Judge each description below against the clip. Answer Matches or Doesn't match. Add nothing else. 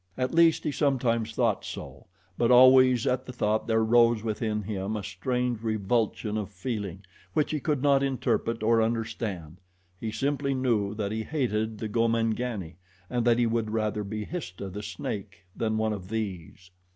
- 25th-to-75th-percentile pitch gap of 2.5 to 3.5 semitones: Matches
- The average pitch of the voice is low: Matches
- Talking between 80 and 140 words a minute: Doesn't match